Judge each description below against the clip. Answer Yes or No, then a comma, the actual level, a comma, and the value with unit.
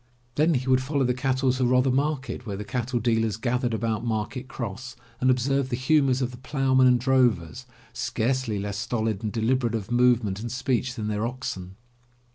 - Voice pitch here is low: Yes, low, 125 Hz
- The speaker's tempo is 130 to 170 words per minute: No, average, 185 wpm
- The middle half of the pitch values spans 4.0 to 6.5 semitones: No, narrow, 2.6 semitones